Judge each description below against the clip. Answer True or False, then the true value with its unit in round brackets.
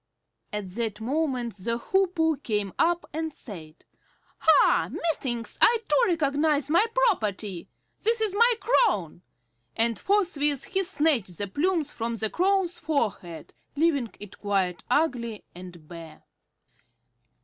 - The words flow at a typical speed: False (125 wpm)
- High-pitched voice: True (275 Hz)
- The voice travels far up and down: True (8.3 semitones)